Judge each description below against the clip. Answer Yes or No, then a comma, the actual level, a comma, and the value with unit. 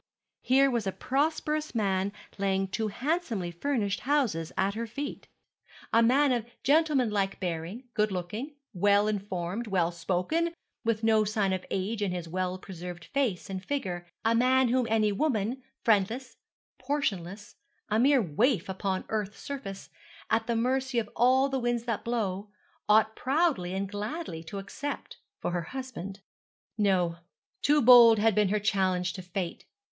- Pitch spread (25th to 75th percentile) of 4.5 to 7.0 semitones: Yes, average, 4.9 semitones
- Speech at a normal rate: Yes, average, 150 wpm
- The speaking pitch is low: No, high, 215 Hz